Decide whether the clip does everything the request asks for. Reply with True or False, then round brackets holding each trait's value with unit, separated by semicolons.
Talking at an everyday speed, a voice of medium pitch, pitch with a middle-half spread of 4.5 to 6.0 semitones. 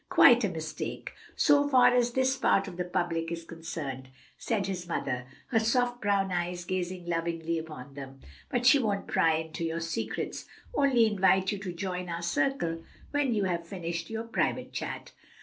True (175 wpm; 180 Hz; 5.2 semitones)